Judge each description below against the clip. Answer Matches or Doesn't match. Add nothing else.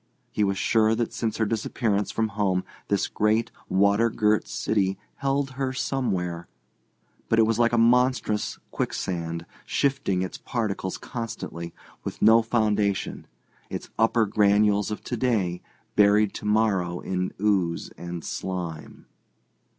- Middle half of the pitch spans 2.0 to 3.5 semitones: Matches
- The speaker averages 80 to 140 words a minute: Matches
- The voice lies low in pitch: Matches